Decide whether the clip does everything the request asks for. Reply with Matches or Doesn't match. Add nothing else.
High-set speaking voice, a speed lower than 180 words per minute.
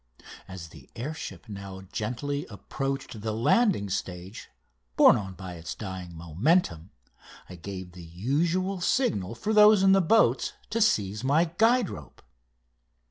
Doesn't match